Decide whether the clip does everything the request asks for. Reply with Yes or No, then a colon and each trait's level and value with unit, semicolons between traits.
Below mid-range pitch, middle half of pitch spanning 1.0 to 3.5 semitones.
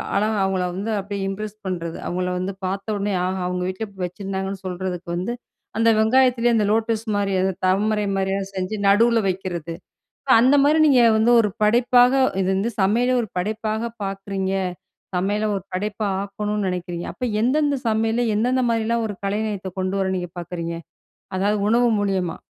No: high, 200 Hz; average, 3.0 semitones